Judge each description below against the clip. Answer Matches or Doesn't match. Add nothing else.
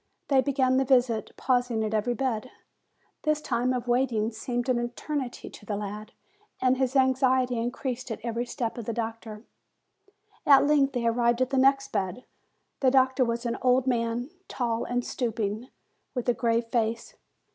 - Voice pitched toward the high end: Matches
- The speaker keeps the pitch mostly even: Matches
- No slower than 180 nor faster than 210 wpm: Doesn't match